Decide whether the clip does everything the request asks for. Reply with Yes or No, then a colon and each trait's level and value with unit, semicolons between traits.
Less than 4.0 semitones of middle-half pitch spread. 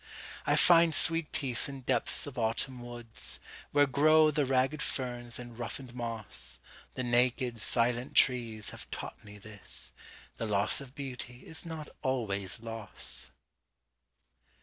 Yes: average, 3.2 semitones